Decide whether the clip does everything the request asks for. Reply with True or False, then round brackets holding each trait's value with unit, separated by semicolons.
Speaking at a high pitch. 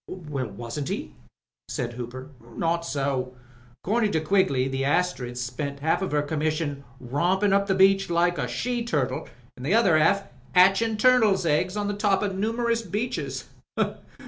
False (170 Hz)